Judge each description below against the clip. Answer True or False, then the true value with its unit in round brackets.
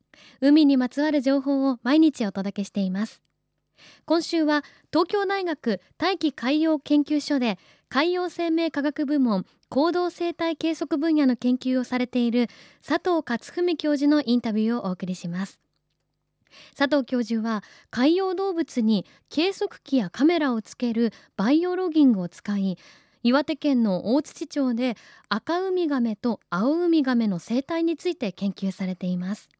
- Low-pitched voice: False (275 Hz)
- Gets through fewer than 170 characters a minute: False (290 characters per minute)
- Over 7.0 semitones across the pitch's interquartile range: False (6.0 semitones)